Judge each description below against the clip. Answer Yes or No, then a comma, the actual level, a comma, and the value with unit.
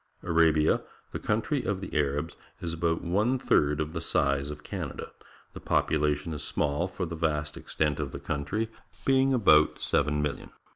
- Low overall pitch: Yes, very low, 80 Hz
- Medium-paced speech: Yes, average, 165 wpm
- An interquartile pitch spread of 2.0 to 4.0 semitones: Yes, average, 3.7 semitones